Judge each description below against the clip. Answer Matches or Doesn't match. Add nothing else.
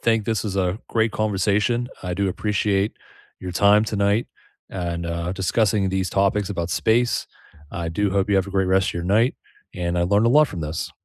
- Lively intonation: Doesn't match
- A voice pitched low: Matches